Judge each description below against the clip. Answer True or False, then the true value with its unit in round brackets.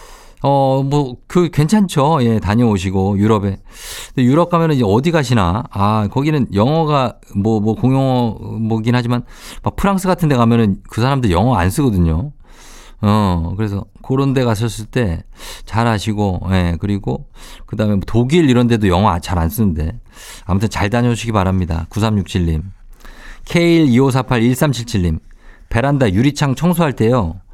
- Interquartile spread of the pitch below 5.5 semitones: True (5.1 semitones)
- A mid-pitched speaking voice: False (115 Hz)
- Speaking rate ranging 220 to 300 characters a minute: True (280 characters per minute)